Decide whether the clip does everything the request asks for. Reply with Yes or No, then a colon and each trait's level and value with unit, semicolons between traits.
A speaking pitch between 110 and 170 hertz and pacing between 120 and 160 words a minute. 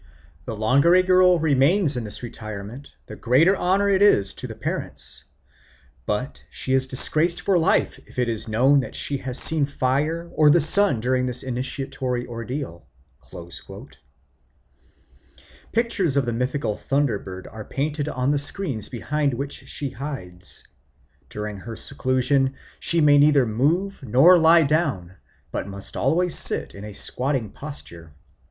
Yes: low, 135 Hz; average, 150 wpm